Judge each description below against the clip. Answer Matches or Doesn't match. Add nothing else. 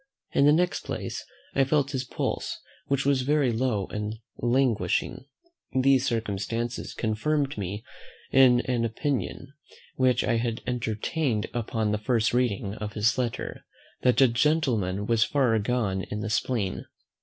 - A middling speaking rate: Matches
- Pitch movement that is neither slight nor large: Matches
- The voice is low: Matches